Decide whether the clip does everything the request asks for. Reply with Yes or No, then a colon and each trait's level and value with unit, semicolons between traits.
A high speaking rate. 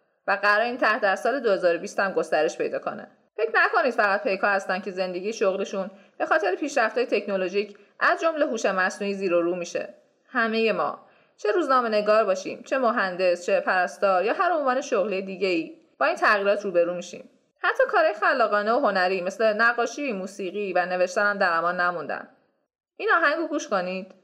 Yes: fast, 175 wpm